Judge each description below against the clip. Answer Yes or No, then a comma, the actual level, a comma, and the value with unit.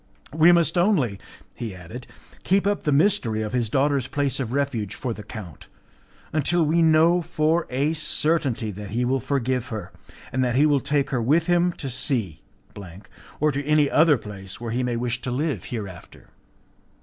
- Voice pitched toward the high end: No, low, 135 Hz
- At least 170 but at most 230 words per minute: Yes, average, 180 wpm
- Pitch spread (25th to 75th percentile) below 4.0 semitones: No, average, 5.0 semitones